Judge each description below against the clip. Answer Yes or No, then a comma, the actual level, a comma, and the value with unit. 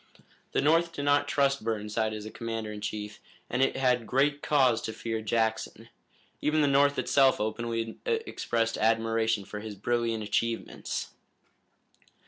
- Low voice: Yes, low, 115 Hz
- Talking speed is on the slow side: No, average, 145 wpm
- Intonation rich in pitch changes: No, average, 3.9 semitones